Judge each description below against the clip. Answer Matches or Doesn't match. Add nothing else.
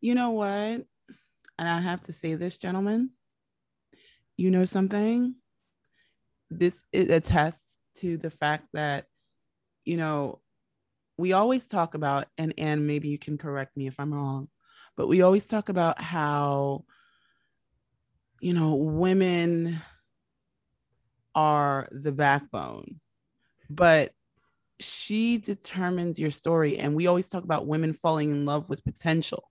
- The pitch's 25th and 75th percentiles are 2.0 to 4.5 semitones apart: Matches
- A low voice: Doesn't match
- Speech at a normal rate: Doesn't match